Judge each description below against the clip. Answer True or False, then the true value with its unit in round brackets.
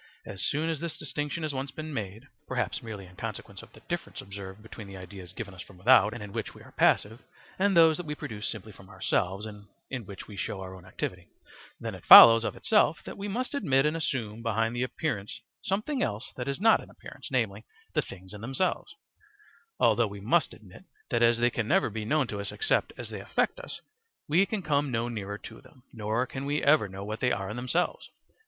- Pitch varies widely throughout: True (6.4 semitones)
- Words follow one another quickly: True (225 wpm)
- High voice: False (115 Hz)